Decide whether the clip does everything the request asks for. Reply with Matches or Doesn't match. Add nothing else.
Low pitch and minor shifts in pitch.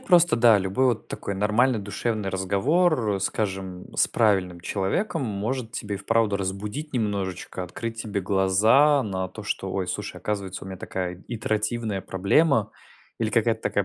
Doesn't match